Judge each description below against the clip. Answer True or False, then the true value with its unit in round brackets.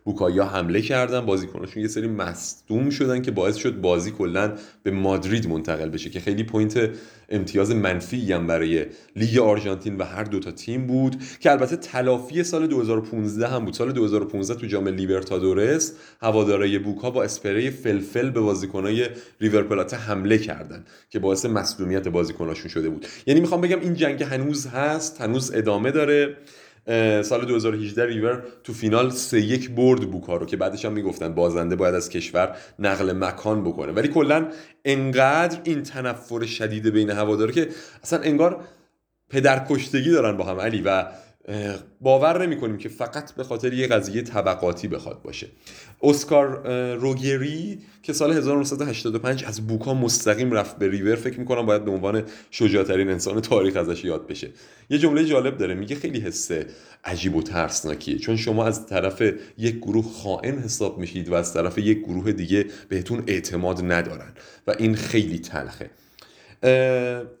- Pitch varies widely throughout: False (4.8 semitones)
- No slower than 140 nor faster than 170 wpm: True (155 wpm)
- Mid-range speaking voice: False (110 Hz)